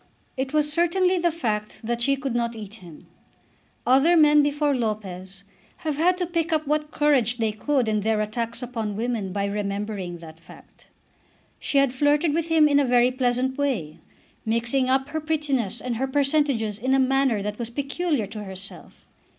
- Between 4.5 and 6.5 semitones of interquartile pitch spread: Yes, wide, 5.4 semitones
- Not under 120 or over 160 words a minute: No, average, 180 wpm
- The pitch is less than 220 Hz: No, very high, 255 Hz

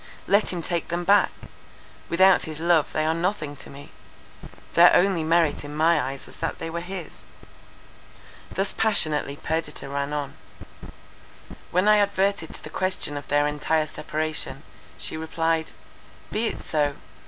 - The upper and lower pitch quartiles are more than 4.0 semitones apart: No, average, 3.5 semitones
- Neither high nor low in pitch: Yes, medium, 160 Hz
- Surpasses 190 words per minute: No, average, 155 wpm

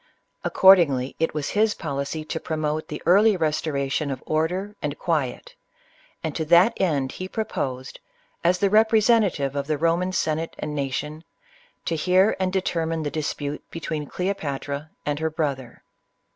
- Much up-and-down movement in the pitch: No, average, 4.2 semitones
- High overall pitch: No, medium, 160 Hz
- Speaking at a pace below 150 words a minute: No, average, 155 wpm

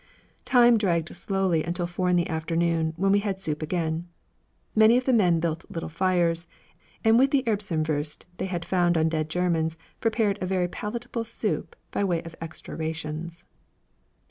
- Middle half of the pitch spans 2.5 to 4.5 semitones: Yes, average, 3.8 semitones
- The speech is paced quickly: No, average, 170 wpm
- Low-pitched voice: No, medium, 175 Hz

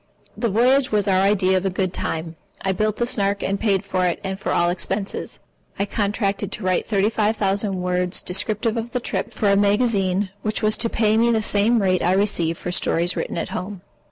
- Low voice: No, high, 200 Hz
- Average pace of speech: No, fast, 215 wpm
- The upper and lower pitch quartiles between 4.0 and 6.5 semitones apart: No, narrow, 2.4 semitones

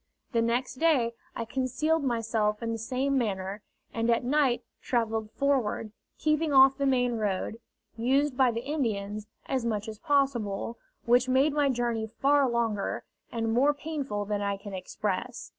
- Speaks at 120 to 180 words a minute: Yes, average, 160 wpm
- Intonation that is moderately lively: Yes, average, 3.7 semitones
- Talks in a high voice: Yes, high, 235 Hz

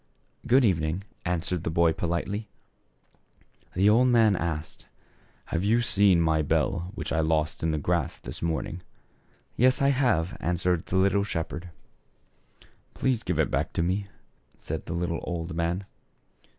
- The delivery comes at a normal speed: Yes, average, 160 wpm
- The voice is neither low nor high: No, very low, 90 Hz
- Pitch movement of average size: Yes, average, 3.7 semitones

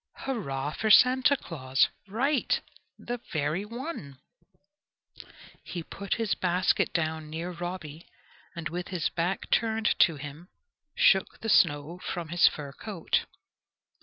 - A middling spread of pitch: No, wide, 5.8 semitones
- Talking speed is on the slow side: Yes, slow, 125 wpm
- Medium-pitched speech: Yes, medium, 175 Hz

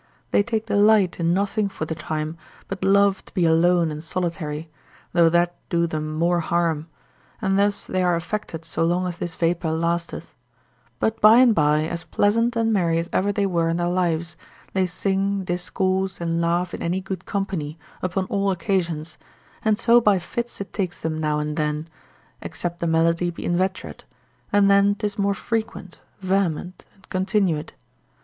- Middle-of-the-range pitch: Yes, medium, 180 Hz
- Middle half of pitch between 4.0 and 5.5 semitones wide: No, average, 3.1 semitones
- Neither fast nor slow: Yes, average, 175 wpm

